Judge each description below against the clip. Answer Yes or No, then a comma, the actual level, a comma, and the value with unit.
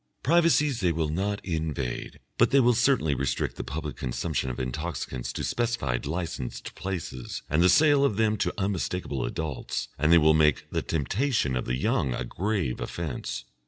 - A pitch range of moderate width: No, wide, 7.5 semitones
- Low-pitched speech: Yes, very low, 80 Hz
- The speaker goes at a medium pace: Yes, average, 170 wpm